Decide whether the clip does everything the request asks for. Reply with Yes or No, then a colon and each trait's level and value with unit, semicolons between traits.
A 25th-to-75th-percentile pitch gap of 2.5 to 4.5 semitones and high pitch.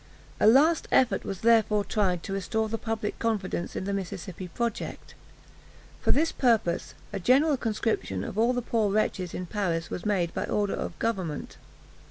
Yes: average, 3.7 semitones; high, 210 Hz